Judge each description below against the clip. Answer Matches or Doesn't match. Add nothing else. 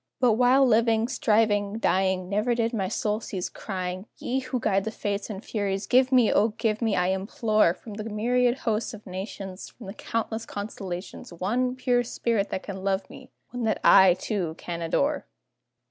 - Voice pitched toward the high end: Matches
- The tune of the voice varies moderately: Matches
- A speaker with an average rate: Matches